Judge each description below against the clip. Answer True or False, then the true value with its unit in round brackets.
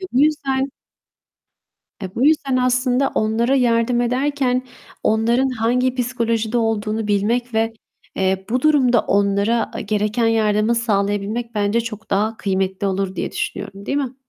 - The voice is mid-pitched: False (230 Hz)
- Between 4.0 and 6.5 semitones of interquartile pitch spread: False (3.4 semitones)